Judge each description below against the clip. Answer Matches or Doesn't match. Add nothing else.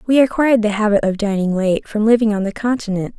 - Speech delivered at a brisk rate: Matches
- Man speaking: Doesn't match